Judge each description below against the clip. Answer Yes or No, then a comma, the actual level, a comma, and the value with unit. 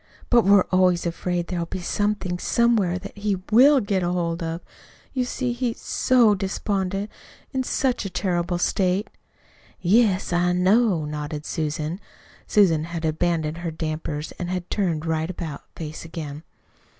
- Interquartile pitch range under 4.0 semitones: Yes, average, 3.6 semitones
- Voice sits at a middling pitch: Yes, medium, 180 Hz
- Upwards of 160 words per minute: No, average, 145 wpm